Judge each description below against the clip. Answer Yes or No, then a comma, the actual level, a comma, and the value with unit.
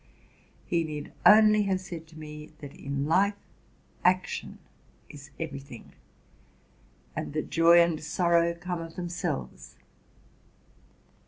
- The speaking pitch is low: No, medium, 165 Hz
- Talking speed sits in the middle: No, slow, 115 wpm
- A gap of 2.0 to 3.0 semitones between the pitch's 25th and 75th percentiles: Yes, average, 2.7 semitones